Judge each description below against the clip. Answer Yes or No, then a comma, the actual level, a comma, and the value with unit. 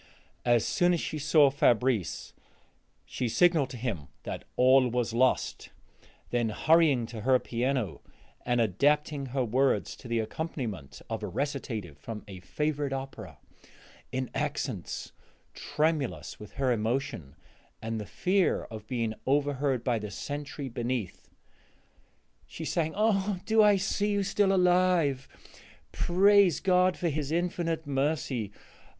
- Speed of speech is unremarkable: No, slow, 130 wpm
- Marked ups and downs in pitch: Yes, wide, 5.7 semitones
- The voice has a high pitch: No, low, 135 Hz